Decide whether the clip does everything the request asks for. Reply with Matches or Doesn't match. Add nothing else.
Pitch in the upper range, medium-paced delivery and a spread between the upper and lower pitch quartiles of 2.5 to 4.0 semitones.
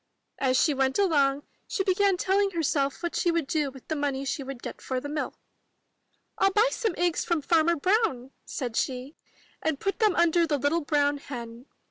Doesn't match